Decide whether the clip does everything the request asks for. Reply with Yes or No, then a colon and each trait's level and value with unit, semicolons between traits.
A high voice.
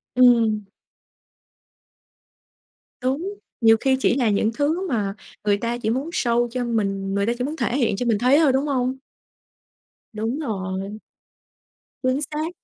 Yes: high, 240 Hz